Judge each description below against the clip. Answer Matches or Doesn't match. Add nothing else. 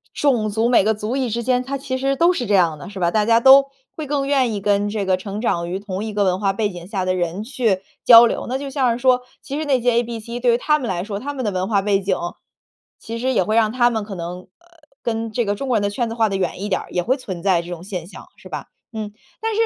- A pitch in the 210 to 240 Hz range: Matches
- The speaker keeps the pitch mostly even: Doesn't match